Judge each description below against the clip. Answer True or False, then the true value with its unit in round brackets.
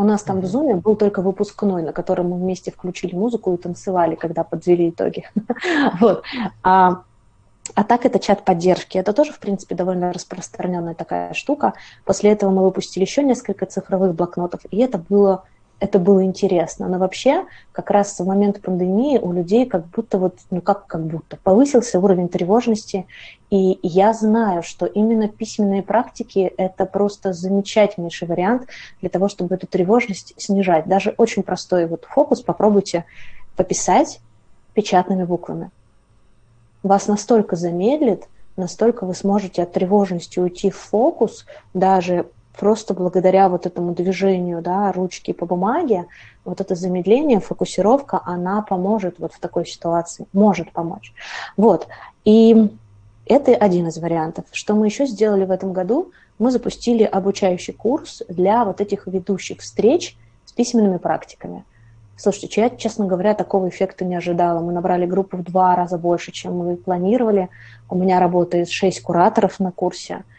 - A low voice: False (190 Hz)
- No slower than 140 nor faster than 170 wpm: True (150 wpm)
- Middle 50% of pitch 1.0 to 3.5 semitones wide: True (2.8 semitones)